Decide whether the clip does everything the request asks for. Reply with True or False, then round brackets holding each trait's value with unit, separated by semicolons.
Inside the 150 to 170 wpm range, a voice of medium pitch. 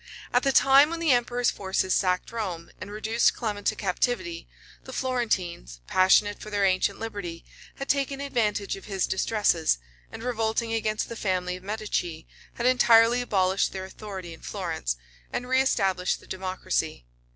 False (155 wpm; 210 Hz)